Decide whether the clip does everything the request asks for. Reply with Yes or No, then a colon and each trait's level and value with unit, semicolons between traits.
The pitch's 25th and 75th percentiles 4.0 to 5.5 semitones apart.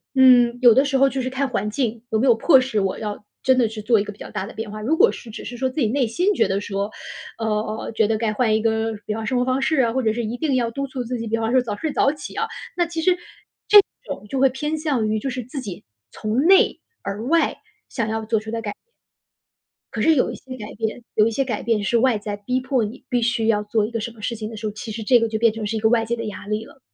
No: average, 3.3 semitones